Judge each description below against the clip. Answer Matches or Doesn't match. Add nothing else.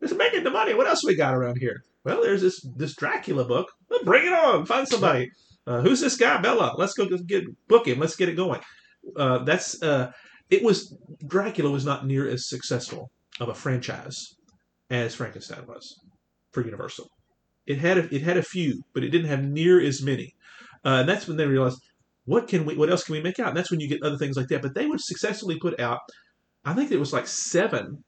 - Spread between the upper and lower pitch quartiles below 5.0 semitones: Doesn't match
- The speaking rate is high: Matches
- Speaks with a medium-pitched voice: Matches